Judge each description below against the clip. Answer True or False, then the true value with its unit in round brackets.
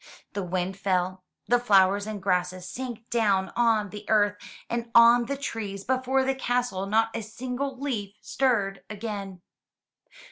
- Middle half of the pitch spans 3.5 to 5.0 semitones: True (3.8 semitones)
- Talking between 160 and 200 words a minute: False (145 wpm)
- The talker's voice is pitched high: True (215 Hz)